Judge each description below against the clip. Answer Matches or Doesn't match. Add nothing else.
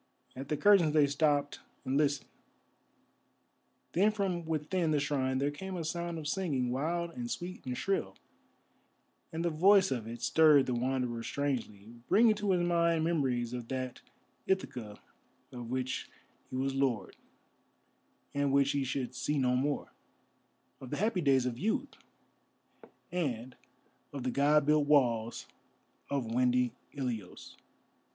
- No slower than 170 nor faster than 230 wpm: Doesn't match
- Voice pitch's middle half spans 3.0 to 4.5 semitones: Doesn't match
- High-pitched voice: Doesn't match